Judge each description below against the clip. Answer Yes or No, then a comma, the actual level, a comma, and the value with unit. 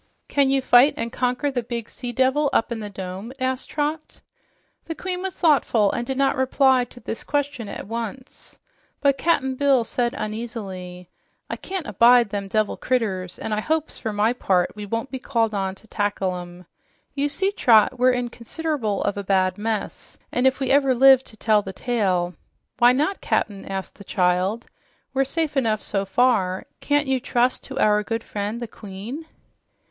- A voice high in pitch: Yes, high, 235 Hz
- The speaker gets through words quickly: No, average, 185 wpm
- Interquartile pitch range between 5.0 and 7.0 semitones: No, average, 4.6 semitones